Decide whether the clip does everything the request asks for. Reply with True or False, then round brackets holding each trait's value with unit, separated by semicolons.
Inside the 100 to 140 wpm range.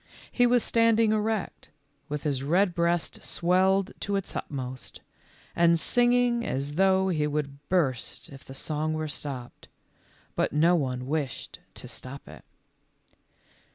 True (135 wpm)